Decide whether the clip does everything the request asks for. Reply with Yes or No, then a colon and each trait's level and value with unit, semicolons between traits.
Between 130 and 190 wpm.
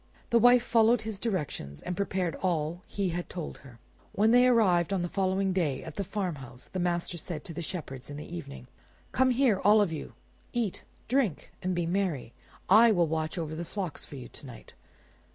No: fast, 205 wpm